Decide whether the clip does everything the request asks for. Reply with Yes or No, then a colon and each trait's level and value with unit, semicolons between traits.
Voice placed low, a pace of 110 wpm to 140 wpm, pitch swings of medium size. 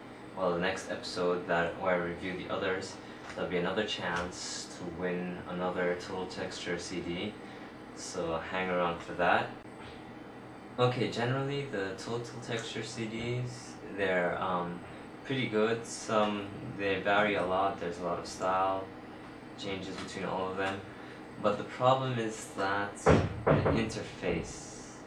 Yes: very low, 95 Hz; slow, 135 wpm; average, 3.5 semitones